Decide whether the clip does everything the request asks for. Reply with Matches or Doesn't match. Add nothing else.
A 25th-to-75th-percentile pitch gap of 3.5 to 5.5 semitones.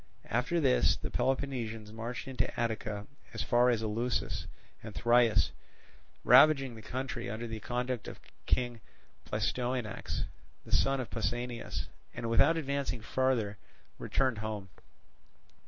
Doesn't match